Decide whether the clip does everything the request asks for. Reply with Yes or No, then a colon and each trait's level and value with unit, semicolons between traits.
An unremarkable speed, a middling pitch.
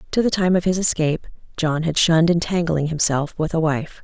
No: fast, 225 wpm; medium, 165 Hz